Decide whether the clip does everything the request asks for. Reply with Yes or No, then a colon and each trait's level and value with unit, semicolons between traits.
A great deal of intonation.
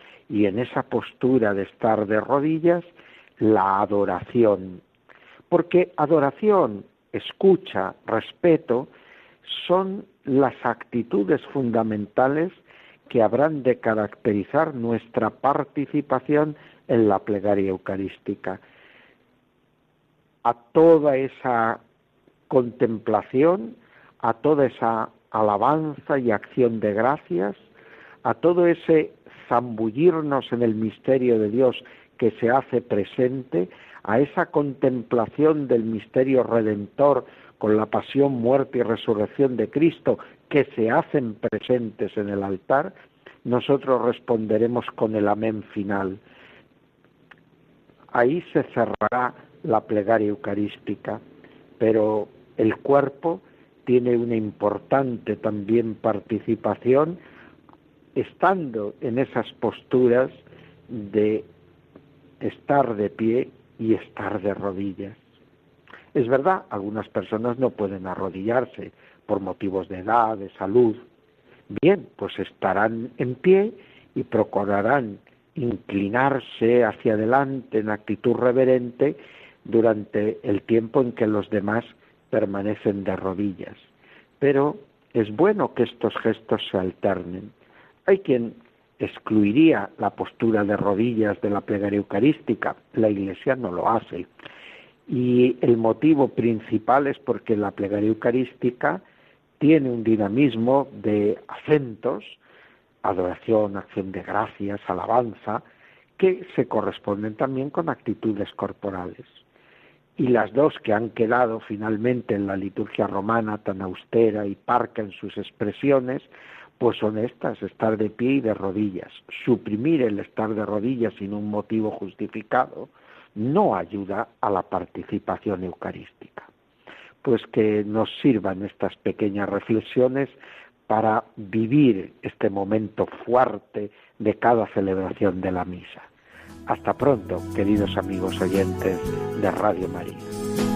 No: average, 4.0 semitones